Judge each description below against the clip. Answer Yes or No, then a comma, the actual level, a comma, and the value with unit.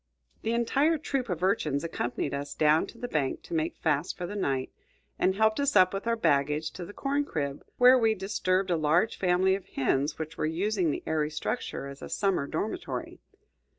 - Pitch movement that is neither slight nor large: No, wide, 6.3 semitones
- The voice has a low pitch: No, medium, 180 Hz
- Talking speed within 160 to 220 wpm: Yes, average, 200 wpm